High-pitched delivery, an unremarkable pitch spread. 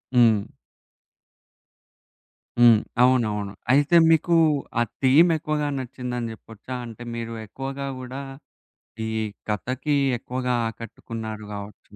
No: low, 120 Hz; average, 3.1 semitones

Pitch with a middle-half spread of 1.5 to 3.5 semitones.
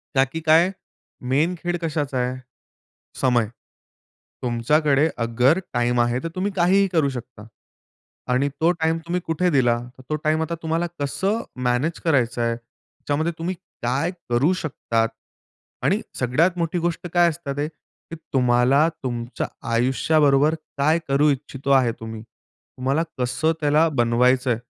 No: average, 4.8 semitones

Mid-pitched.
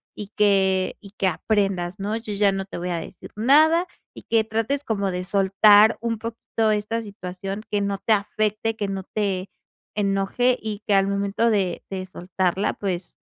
No: high, 200 Hz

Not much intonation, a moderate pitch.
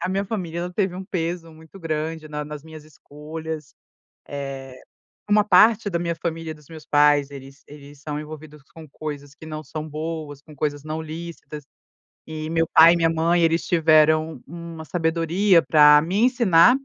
Yes: narrow, 1.9 semitones; medium, 160 Hz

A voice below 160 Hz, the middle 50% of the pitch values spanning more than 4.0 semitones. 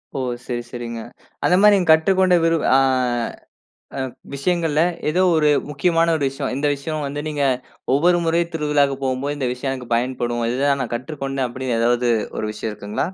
Yes: medium, 140 Hz; average, 4.4 semitones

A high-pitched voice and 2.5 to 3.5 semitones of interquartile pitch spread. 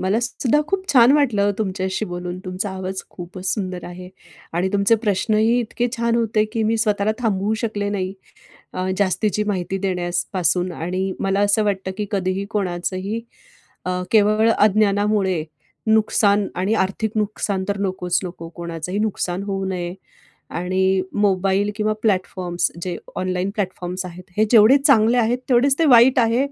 Yes: high, 200 Hz; average, 2.8 semitones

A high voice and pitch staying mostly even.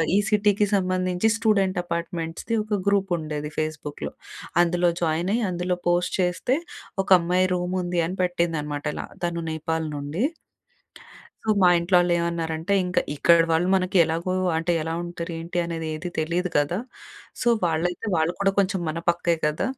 No: medium, 175 Hz; narrow, 2.1 semitones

